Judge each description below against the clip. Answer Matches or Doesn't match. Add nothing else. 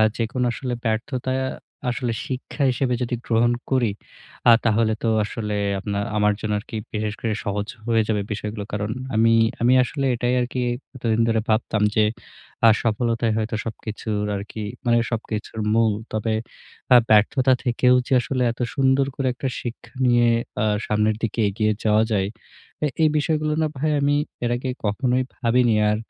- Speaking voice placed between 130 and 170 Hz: Doesn't match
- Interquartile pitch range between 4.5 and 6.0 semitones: Doesn't match